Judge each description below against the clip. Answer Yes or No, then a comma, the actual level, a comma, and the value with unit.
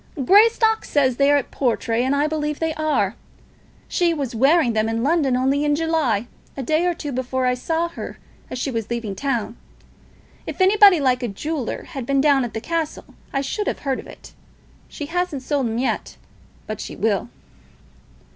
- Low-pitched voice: No, very high, 275 Hz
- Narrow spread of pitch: No, average, 4.8 semitones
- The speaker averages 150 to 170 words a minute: No, average, 190 wpm